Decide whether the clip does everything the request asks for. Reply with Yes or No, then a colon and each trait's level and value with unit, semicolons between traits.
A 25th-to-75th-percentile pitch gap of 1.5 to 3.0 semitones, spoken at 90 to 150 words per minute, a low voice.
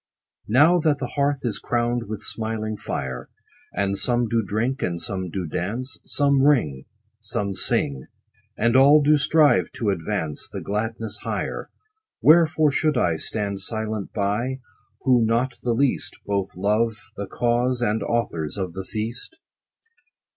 No: average, 4.6 semitones; average, 145 wpm; low, 115 Hz